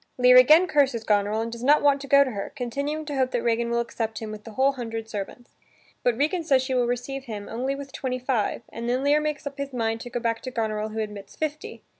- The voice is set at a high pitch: Yes, high, 245 Hz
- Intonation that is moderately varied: Yes, average, 3.6 semitones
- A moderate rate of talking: No, fast, 255 wpm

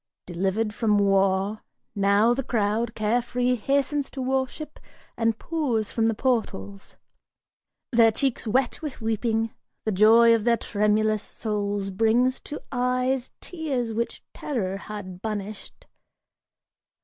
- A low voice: No, high, 225 Hz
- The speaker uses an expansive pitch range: No, average, 3.2 semitones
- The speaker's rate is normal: No, slow, 120 wpm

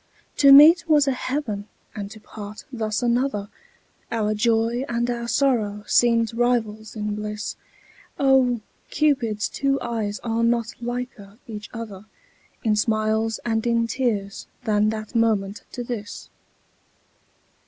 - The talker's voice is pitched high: Yes, high, 225 Hz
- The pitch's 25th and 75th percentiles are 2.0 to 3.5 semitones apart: Yes, narrow, 2.4 semitones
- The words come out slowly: Yes, slow, 130 wpm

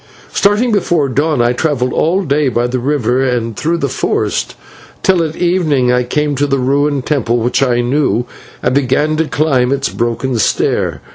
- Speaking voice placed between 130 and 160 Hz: Yes, medium, 140 Hz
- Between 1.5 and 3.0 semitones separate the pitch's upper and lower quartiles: No, average, 3.6 semitones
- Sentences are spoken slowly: No, average, 185 wpm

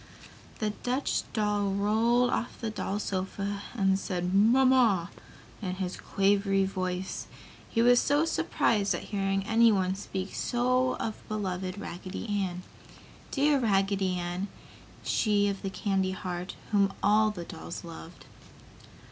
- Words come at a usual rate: No, slow, 130 wpm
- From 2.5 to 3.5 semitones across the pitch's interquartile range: Yes, average, 2.8 semitones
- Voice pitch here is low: No, high, 200 Hz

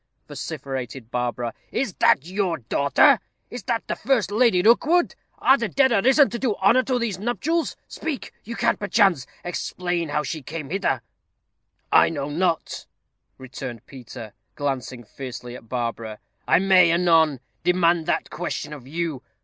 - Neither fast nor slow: Yes, average, 150 wpm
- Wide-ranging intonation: Yes, wide, 8.5 semitones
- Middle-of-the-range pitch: Yes, medium, 170 Hz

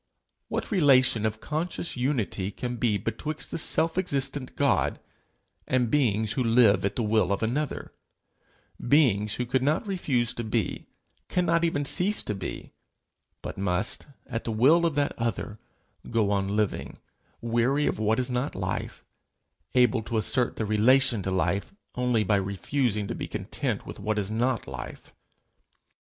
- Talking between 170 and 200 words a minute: No, average, 155 wpm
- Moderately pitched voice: No, low, 120 Hz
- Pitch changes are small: No, average, 4.7 semitones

